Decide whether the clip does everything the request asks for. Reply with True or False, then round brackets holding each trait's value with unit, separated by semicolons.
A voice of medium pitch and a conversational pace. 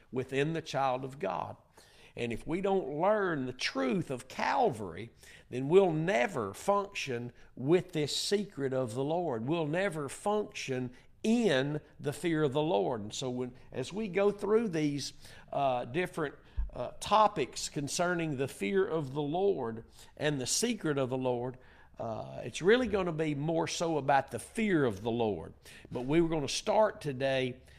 True (150 Hz; 170 wpm)